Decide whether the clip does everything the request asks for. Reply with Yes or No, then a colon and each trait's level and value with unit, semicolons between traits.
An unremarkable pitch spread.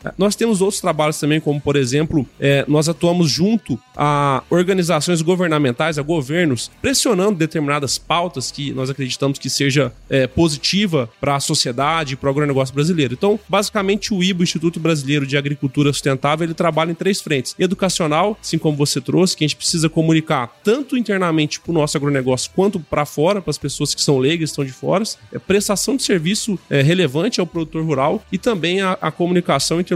Yes: average, 4.3 semitones